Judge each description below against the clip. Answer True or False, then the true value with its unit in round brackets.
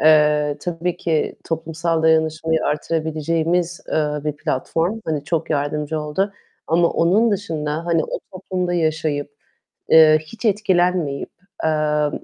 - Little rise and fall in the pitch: True (2.3 semitones)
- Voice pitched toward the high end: False (160 Hz)